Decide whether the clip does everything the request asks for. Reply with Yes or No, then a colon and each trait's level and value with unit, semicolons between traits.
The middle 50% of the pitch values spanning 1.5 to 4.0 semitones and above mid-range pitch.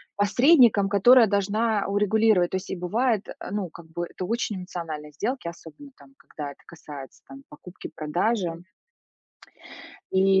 No: average, 4.4 semitones; high, 195 Hz